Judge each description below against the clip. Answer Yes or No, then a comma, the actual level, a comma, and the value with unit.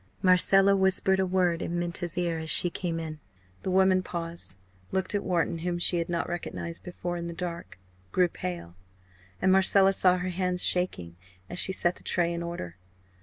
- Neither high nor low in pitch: Yes, medium, 175 Hz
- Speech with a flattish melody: Yes, narrow, 1.7 semitones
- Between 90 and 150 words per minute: No, average, 185 wpm